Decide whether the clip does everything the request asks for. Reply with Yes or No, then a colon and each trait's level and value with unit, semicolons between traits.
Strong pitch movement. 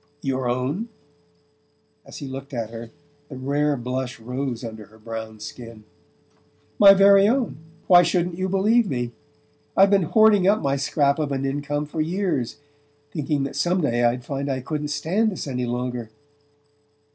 Yes: wide, 6.3 semitones